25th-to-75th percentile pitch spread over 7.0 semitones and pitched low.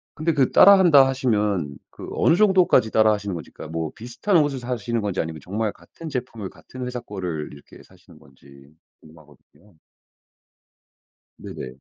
Yes: wide, 8.4 semitones; low, 110 Hz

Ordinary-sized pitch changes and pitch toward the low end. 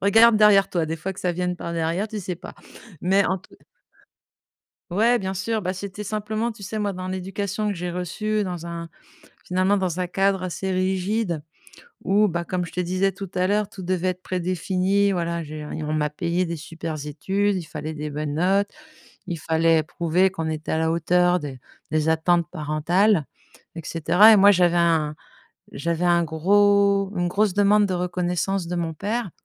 No: average, 3.0 semitones; medium, 180 Hz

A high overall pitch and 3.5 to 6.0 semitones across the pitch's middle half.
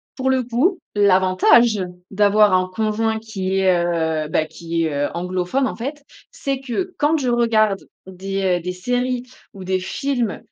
Yes: high, 205 Hz; average, 5.0 semitones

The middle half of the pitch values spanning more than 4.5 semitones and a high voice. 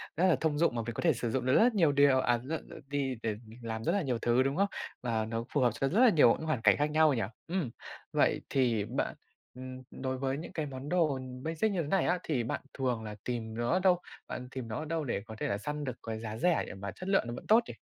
No: average, 5.2 semitones; low, 130 Hz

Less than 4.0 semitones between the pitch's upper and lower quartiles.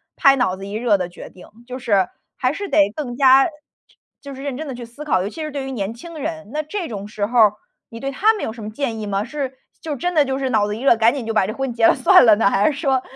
No: average, 4.7 semitones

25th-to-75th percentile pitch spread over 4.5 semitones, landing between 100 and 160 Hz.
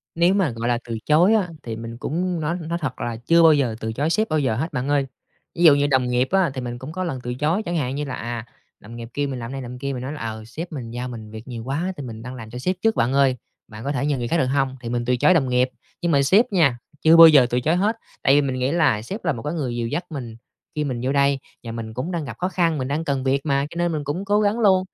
Yes: average, 5.1 semitones; medium, 140 Hz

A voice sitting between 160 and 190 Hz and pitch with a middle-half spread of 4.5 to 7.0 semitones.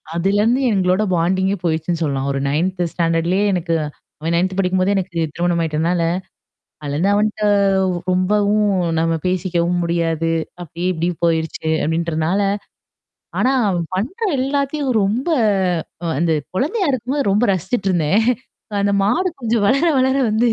No: medium, 185 Hz; average, 3.9 semitones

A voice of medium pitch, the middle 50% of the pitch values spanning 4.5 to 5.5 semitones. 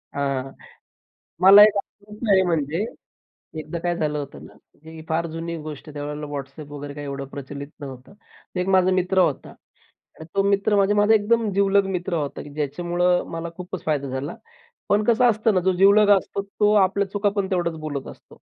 Yes: medium, 175 Hz; average, 5.2 semitones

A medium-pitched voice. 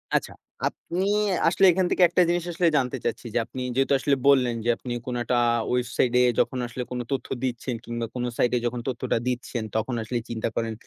No: low, 125 Hz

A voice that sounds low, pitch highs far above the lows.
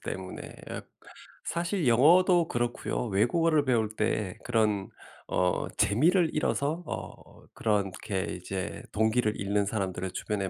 Yes: low, 110 Hz; wide, 7.7 semitones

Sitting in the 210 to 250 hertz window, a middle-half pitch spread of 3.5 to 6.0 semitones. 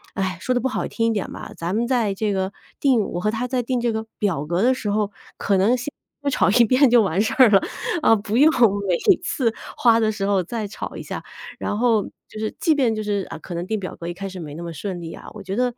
Yes: high, 215 Hz; average, 3.9 semitones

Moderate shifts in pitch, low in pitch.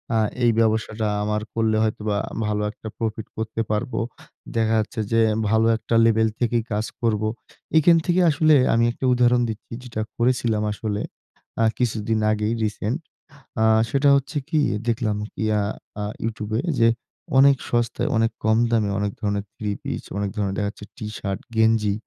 No: narrow, 1.8 semitones; low, 110 Hz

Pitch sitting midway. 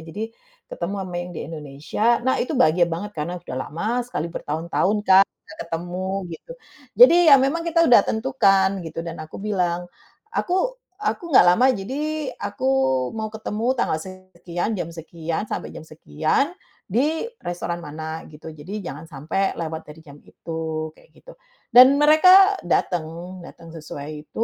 Yes: medium, 175 Hz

